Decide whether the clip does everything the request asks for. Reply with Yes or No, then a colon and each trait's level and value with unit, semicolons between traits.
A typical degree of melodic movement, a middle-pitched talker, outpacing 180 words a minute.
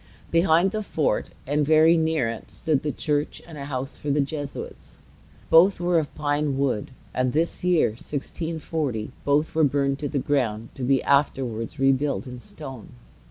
No: average, 3.0 semitones; medium, 145 Hz; average, 165 wpm